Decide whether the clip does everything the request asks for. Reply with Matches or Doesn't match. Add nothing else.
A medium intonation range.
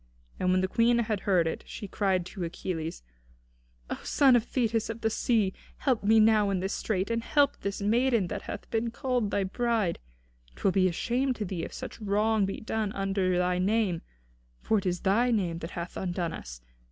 Matches